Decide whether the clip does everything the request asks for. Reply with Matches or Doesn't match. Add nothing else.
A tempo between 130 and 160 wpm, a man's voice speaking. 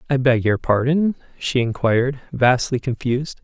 Matches